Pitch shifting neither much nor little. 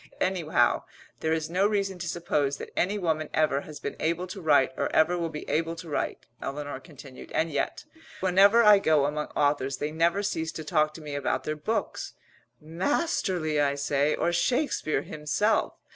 Yes: average, 3.5 semitones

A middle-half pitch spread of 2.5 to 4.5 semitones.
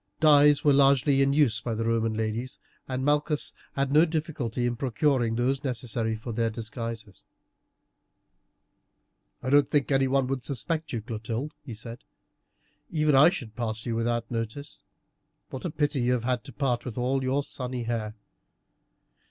Yes: average, 3.5 semitones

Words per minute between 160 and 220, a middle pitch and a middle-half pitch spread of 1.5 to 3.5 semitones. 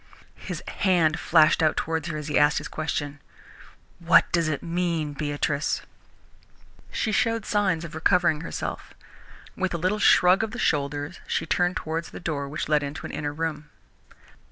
Yes: average, 165 wpm; medium, 160 Hz; average, 3.1 semitones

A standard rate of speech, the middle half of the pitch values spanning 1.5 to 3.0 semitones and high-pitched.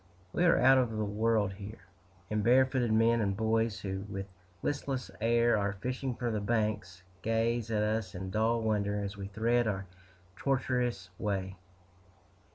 No: average, 160 wpm; average, 2.7 semitones; low, 110 Hz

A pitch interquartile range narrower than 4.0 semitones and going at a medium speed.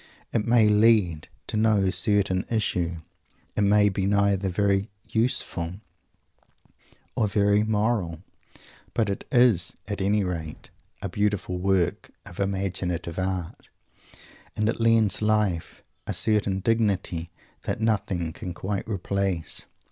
No: average, 2.7 semitones; slow, 120 wpm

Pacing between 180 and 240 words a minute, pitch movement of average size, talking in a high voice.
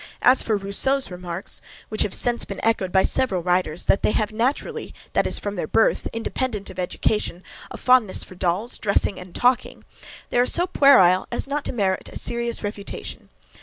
Yes: average, 185 wpm; average, 4.6 semitones; high, 210 Hz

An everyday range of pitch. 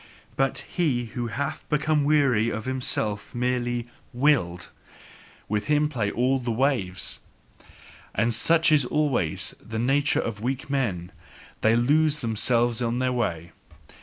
Yes: average, 4.0 semitones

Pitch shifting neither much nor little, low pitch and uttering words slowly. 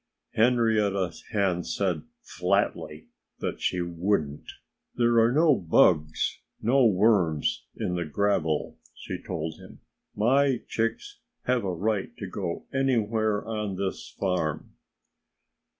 Yes: average, 4.7 semitones; low, 100 Hz; slow, 115 wpm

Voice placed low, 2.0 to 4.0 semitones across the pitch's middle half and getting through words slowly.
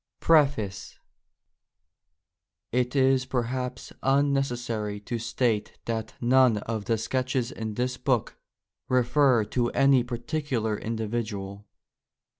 Yes: low, 120 Hz; average, 2.8 semitones; slow, 95 wpm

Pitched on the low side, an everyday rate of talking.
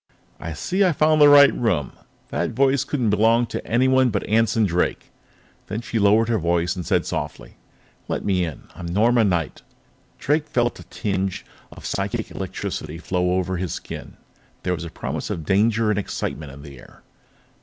Yes: low, 105 Hz; average, 185 wpm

